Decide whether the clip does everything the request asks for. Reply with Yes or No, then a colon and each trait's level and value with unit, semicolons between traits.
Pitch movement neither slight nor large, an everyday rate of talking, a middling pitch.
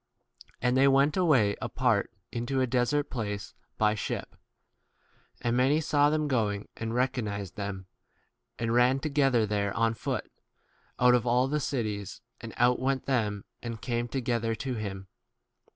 No: average, 3.8 semitones; average, 160 wpm; low, 120 Hz